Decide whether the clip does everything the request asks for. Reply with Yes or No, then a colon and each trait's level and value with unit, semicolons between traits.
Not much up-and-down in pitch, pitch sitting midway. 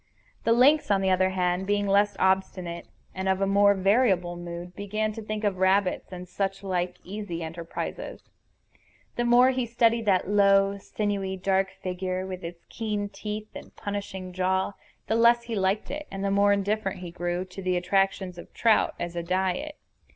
No: narrow, 2.3 semitones; high, 195 Hz